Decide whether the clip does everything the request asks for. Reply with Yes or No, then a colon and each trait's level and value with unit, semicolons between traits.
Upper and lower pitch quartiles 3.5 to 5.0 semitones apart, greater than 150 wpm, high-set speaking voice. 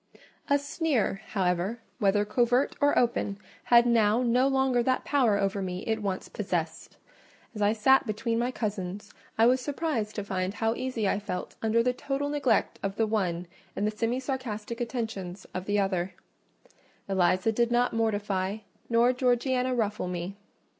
Yes: average, 3.9 semitones; average, 160 wpm; high, 225 Hz